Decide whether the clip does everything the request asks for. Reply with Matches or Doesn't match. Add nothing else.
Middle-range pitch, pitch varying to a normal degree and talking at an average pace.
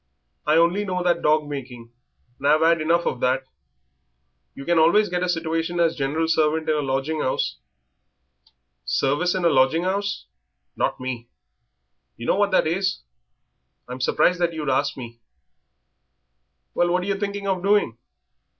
Matches